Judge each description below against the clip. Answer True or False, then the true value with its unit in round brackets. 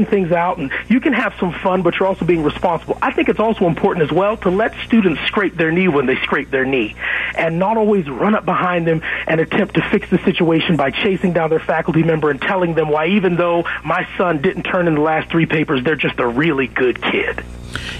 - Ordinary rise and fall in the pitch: True (3.6 semitones)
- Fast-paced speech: True (235 wpm)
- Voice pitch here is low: False (175 Hz)